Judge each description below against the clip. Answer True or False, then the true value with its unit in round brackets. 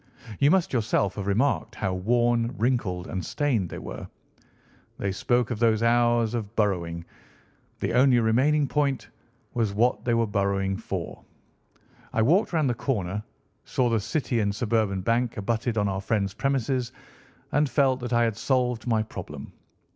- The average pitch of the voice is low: True (115 Hz)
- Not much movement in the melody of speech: False (3.7 semitones)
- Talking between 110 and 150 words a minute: False (160 wpm)